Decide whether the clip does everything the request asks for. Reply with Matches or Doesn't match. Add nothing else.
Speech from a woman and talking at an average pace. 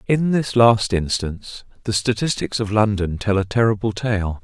Doesn't match